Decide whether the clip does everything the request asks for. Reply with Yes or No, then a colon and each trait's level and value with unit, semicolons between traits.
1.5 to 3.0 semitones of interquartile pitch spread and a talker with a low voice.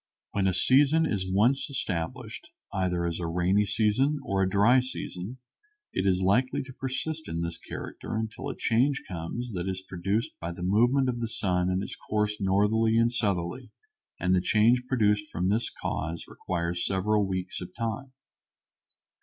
No: average, 4.6 semitones; low, 105 Hz